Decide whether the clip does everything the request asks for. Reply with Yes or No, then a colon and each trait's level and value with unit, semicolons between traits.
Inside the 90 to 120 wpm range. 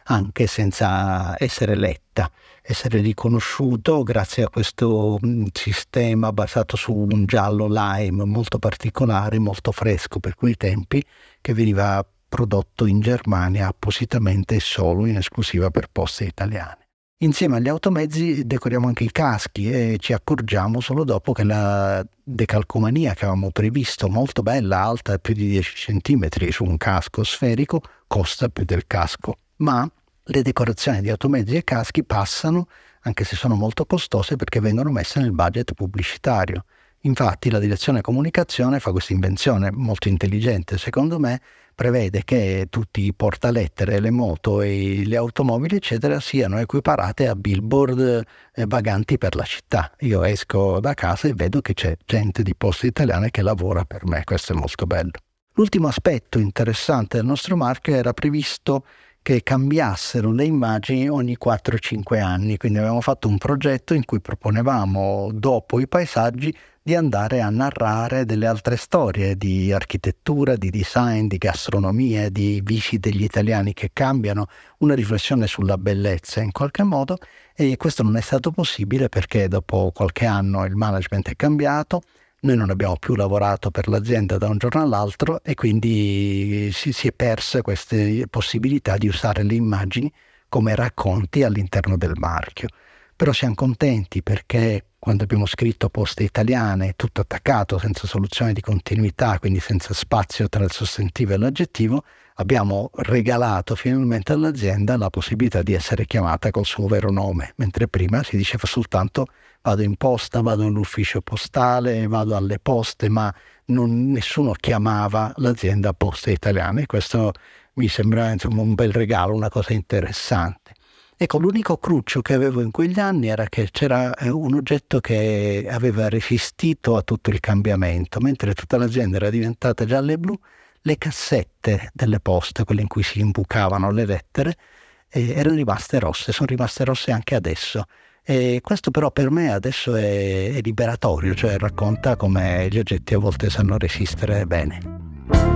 No: average, 150 wpm